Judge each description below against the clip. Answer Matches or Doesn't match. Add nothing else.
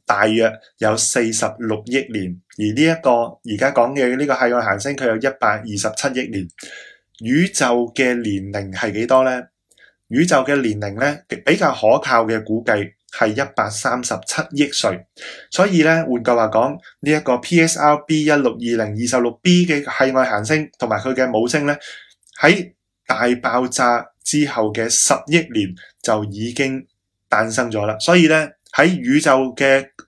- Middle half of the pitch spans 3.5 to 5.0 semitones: Matches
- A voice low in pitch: Matches